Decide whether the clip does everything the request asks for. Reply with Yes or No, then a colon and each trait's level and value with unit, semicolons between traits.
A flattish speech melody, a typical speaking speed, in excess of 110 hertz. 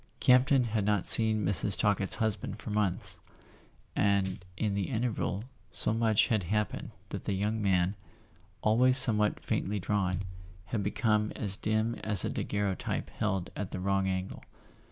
No: narrow, 2.1 semitones; average, 150 wpm; low, 105 Hz